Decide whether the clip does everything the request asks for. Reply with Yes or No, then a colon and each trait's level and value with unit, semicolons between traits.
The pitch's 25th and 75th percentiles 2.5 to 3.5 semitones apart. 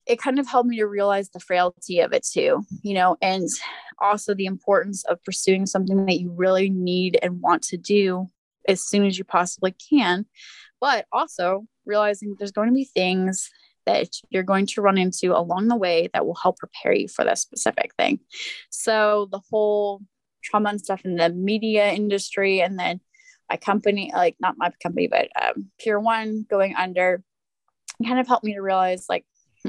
Yes: average, 3.0 semitones